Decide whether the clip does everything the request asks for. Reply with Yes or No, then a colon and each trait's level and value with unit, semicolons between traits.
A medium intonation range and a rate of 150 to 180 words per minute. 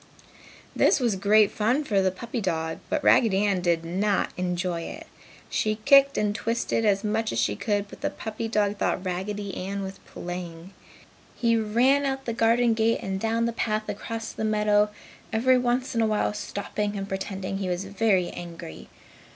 Yes: average, 3.0 semitones; average, 175 wpm